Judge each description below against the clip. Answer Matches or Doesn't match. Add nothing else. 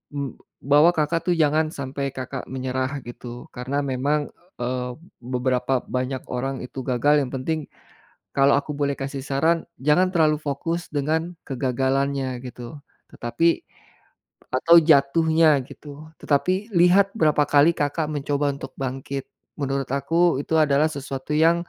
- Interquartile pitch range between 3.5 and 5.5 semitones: Doesn't match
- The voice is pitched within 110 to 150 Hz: Matches